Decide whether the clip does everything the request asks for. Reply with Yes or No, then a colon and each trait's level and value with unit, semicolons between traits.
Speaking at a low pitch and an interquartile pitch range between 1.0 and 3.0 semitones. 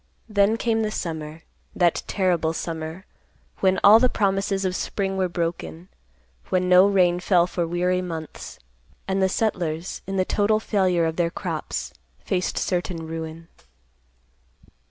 No: medium, 180 Hz; average, 2.7 semitones